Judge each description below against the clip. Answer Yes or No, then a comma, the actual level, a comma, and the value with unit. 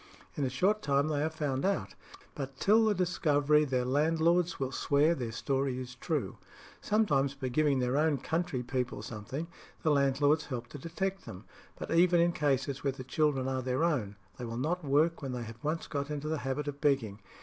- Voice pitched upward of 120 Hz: Yes, medium, 140 Hz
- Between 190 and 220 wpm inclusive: Yes, average, 200 wpm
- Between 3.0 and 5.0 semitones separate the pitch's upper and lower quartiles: Yes, average, 3.6 semitones